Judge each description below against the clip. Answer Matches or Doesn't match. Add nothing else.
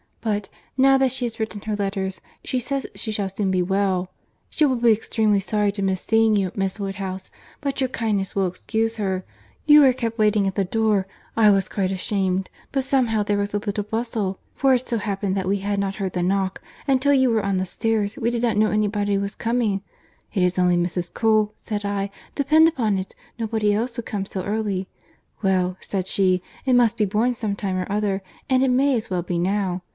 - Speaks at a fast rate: Matches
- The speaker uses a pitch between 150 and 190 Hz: Doesn't match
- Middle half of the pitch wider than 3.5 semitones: Doesn't match